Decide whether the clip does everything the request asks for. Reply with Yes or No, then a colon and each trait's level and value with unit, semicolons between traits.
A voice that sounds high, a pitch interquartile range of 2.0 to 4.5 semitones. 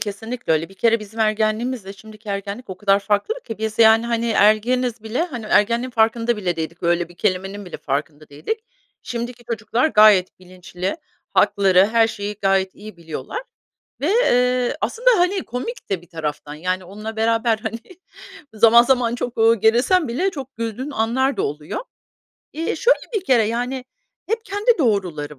Yes: high, 220 Hz; average, 4.2 semitones